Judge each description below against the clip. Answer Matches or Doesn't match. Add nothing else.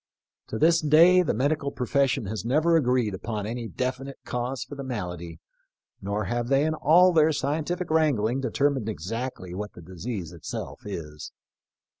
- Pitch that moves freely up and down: Matches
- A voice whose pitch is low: Matches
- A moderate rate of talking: Matches